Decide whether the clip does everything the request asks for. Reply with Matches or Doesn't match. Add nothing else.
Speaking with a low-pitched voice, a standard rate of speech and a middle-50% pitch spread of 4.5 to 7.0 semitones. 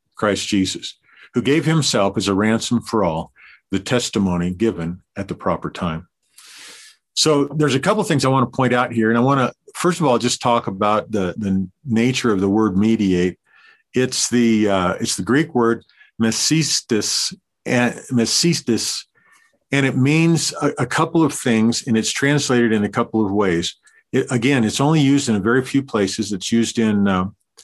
Matches